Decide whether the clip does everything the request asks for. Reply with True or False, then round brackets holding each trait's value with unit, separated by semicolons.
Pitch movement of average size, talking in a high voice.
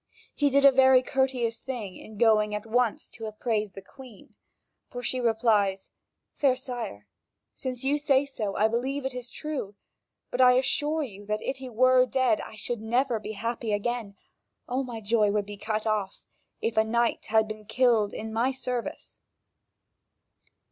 True (3.2 semitones; 235 Hz)